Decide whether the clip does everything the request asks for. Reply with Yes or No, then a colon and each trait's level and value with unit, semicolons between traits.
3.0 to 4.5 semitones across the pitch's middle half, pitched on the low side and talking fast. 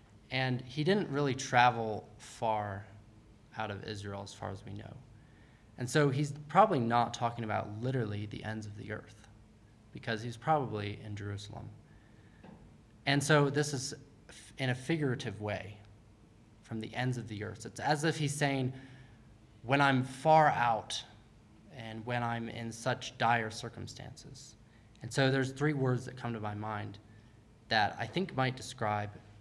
No: average, 3.3 semitones; low, 115 Hz; average, 155 wpm